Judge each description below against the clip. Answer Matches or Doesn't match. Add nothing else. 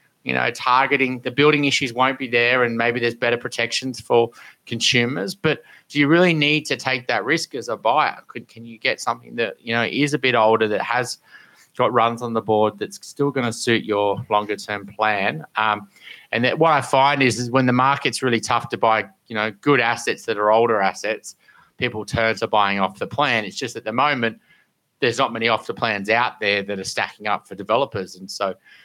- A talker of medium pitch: Doesn't match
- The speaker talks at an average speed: Doesn't match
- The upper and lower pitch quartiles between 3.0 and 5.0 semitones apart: Matches